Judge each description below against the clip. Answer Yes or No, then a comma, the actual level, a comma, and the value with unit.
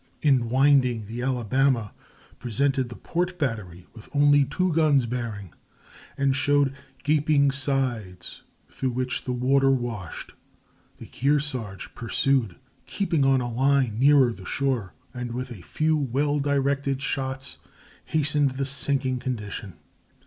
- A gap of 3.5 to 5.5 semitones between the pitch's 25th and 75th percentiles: No, average, 3.0 semitones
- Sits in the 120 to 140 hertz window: Yes, low, 135 Hz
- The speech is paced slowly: Yes, slow, 125 wpm